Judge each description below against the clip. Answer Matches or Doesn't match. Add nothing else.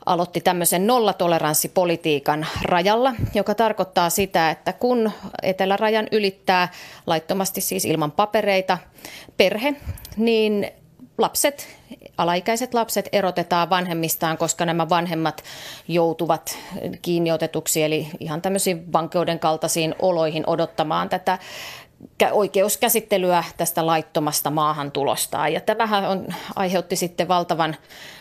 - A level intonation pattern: Doesn't match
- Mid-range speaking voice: Matches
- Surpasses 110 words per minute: Doesn't match